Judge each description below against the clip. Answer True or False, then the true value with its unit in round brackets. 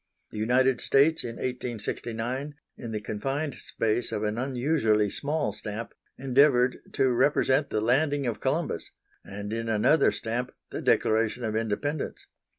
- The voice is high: False (120 Hz)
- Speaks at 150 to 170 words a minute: False (140 wpm)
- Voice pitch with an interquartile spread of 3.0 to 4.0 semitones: True (3.6 semitones)